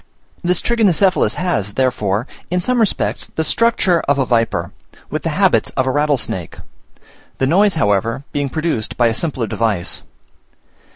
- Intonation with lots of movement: Yes, wide, 7.7 semitones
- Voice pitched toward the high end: No, medium, 140 Hz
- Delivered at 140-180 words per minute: Yes, average, 150 wpm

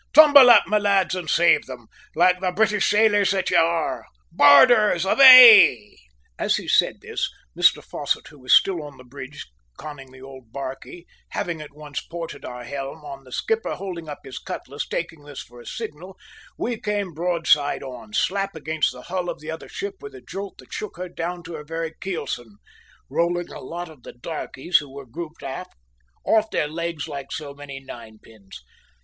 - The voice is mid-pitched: Yes, medium, 165 Hz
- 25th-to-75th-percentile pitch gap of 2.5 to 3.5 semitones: No, wide, 5.5 semitones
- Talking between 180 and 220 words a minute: Yes, average, 185 wpm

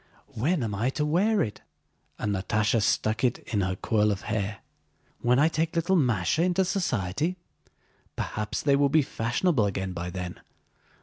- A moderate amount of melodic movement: No, wide, 7.7 semitones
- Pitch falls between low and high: No, low, 115 Hz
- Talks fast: No, average, 165 wpm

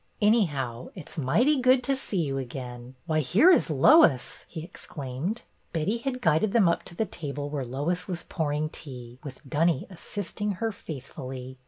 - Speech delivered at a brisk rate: No, average, 180 wpm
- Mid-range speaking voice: Yes, medium, 160 Hz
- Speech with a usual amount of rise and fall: No, wide, 7.5 semitones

